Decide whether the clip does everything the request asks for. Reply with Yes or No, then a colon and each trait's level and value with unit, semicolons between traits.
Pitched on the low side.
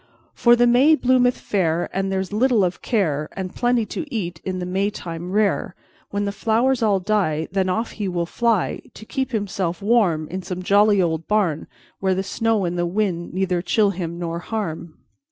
No: high, 195 Hz